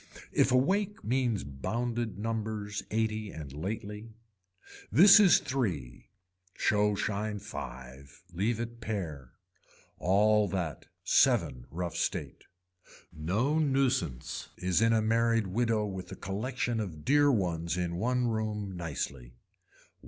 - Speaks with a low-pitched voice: Yes, low, 105 Hz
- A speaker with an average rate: No, slow, 120 wpm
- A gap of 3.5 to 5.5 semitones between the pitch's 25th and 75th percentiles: Yes, average, 5.0 semitones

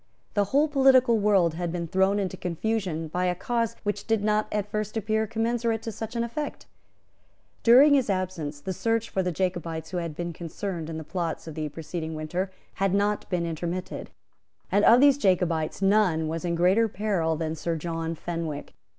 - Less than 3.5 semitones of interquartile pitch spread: No, average, 4.7 semitones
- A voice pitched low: No, medium, 185 Hz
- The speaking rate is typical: Yes, average, 185 wpm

